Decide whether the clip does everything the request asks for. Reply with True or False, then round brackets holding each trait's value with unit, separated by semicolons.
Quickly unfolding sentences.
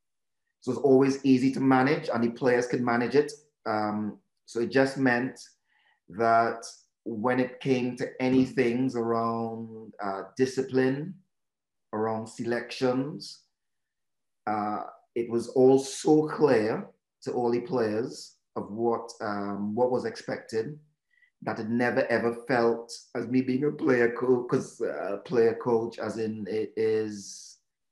False (140 wpm)